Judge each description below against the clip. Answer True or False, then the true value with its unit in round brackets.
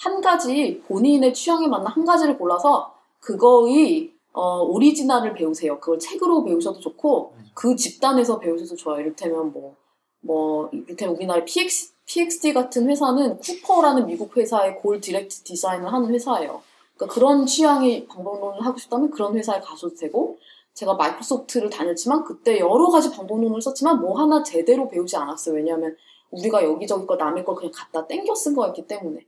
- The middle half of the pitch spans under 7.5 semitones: False (8.4 semitones)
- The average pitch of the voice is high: True (245 Hz)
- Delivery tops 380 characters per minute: True (400 characters per minute)